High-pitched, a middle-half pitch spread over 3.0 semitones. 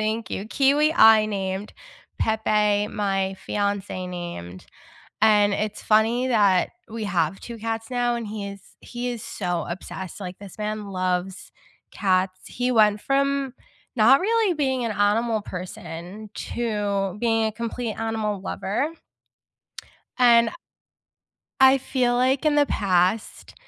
Yes: high, 215 Hz; average, 3.6 semitones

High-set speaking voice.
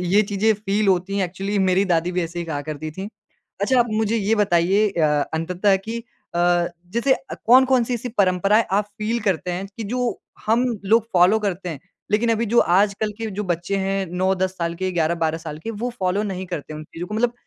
Yes: high, 195 Hz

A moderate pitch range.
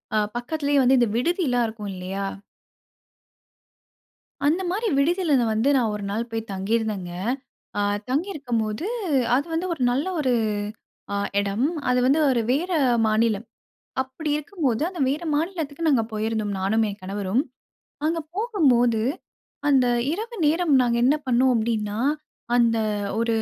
No: wide, 5.7 semitones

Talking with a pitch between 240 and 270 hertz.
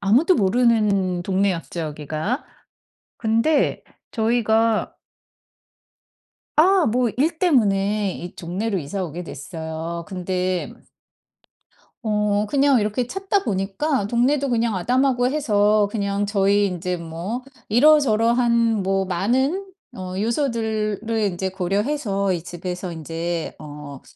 No: high, 205 Hz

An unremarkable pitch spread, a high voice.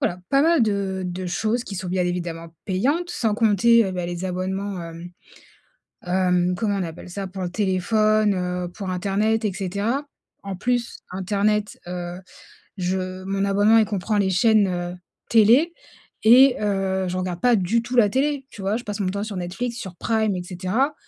Yes: average, 3.4 semitones; high, 195 Hz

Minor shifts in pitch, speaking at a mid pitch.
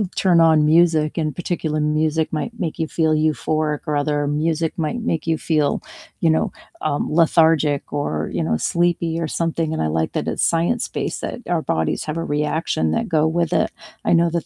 Yes: narrow, 1.7 semitones; medium, 160 Hz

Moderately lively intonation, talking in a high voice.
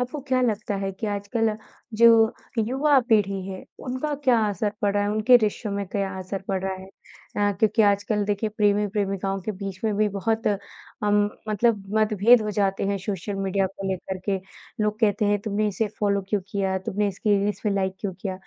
No: narrow, 1.6 semitones; high, 205 Hz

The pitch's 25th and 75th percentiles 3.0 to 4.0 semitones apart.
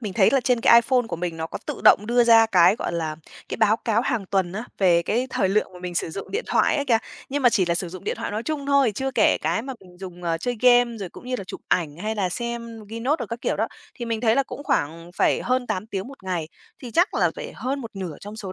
No: average, 5.0 semitones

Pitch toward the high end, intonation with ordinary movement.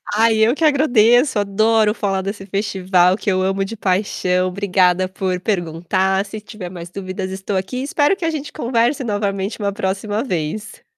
Yes: high, 200 Hz; average, 3.0 semitones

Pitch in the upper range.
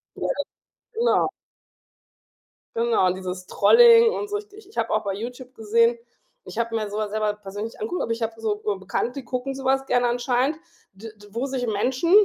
Yes: high, 235 Hz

